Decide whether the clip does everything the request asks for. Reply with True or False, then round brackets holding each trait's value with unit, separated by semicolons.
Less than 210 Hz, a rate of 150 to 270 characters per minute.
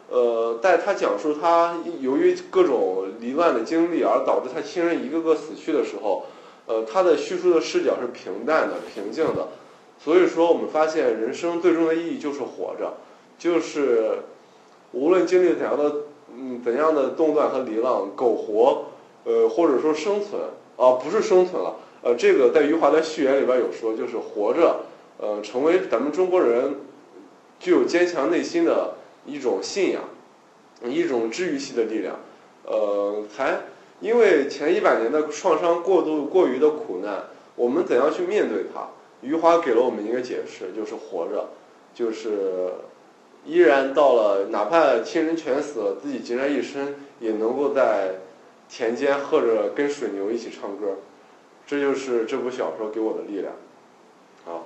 True (185 Hz; 250 characters per minute)